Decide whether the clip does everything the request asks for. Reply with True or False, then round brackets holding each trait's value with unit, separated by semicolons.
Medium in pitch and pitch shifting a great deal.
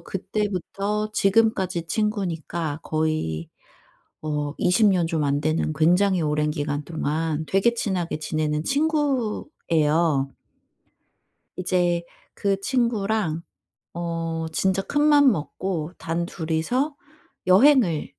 False (175 Hz; 5.0 semitones)